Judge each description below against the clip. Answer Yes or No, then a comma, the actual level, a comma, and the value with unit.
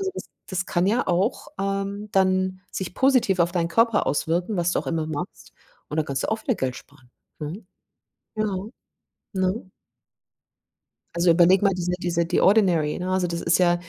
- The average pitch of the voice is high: No, medium, 180 Hz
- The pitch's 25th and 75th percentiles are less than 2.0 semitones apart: No, average, 2.7 semitones